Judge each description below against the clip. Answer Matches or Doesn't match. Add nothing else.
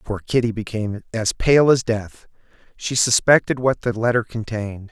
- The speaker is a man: Matches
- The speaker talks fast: Doesn't match